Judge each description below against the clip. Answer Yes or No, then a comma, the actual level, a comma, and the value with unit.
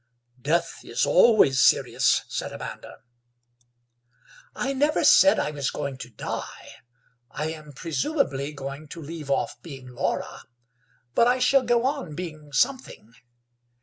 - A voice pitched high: No, medium, 155 Hz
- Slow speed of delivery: Yes, slow, 130 wpm